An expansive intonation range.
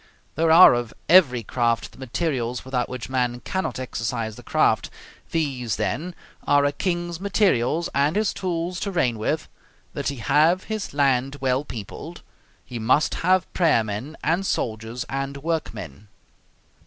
Yes: wide, 5.9 semitones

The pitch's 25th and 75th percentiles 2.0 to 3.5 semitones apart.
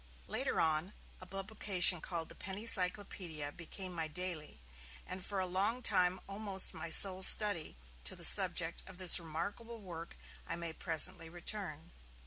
Yes: average, 2.9 semitones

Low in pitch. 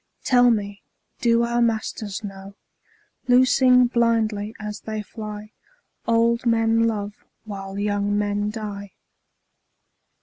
No: high, 215 Hz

